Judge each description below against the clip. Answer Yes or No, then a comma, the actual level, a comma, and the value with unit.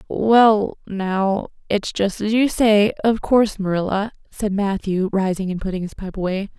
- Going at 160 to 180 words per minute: Yes, average, 165 wpm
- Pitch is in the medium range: No, high, 200 Hz